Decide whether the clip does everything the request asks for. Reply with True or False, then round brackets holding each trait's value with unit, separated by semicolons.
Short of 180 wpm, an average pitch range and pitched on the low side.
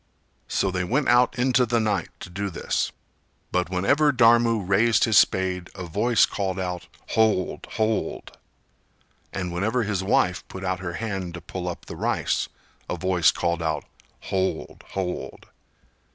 True (150 wpm; 3.7 semitones; 95 Hz)